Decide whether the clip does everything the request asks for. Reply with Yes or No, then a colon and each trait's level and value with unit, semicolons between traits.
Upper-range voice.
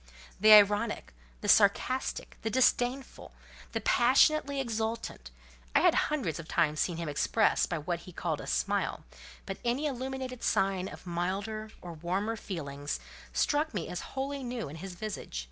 Yes: high, 210 Hz